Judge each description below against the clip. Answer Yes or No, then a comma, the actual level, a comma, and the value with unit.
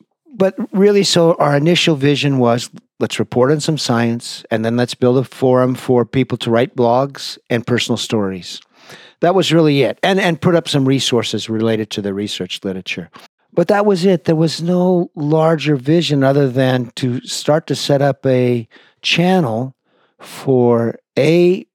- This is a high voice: No, medium, 140 Hz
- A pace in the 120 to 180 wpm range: Yes, average, 170 wpm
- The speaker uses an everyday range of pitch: No, wide, 5.8 semitones